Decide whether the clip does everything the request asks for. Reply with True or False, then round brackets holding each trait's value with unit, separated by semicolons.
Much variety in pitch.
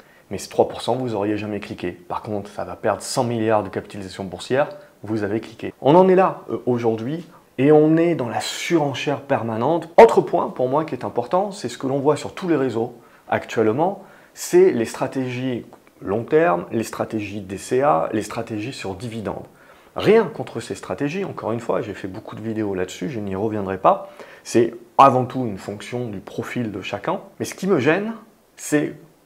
True (5.9 semitones)